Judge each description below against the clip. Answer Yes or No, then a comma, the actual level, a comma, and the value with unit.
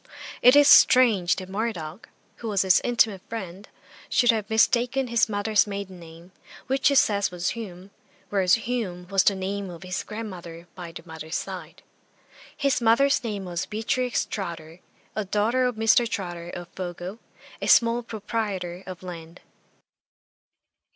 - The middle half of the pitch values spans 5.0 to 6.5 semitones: No, average, 4.4 semitones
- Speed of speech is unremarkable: Yes, average, 150 wpm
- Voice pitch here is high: Yes, high, 200 Hz